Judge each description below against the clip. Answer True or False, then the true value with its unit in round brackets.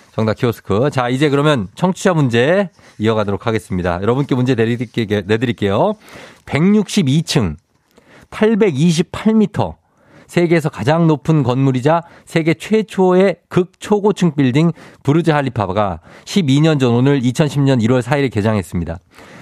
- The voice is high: False (140 Hz)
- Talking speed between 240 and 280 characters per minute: True (270 characters per minute)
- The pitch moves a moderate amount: False (7.1 semitones)